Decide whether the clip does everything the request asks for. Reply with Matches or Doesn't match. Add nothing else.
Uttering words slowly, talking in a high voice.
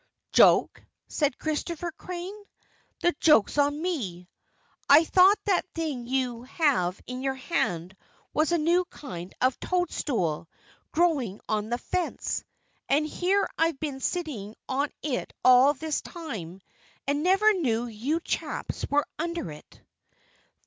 Matches